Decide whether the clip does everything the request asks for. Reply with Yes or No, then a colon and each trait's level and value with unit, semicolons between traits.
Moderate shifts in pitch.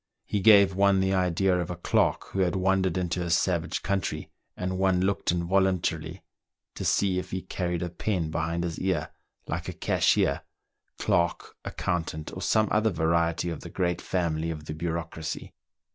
No: narrow, 2.3 semitones